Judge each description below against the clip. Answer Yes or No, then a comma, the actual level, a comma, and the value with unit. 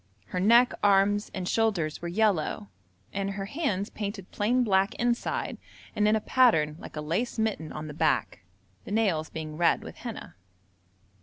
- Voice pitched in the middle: No, high, 200 Hz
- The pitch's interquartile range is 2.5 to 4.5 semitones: No, average, 5.3 semitones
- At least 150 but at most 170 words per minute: Yes, average, 165 wpm